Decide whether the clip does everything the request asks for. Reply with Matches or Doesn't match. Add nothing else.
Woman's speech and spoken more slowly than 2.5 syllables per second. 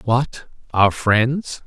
Doesn't match